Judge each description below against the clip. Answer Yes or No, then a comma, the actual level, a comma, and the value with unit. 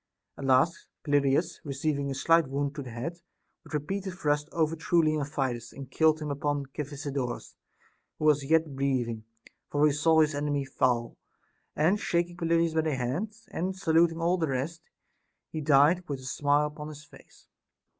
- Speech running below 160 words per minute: No, average, 165 wpm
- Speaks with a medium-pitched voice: Yes, medium, 150 Hz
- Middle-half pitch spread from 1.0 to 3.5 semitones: Yes, average, 3.0 semitones